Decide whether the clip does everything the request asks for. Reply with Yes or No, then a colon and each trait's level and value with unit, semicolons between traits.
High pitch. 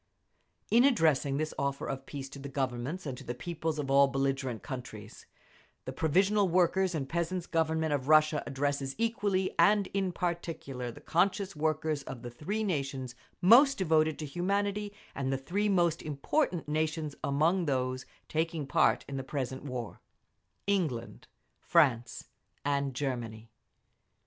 No: medium, 150 Hz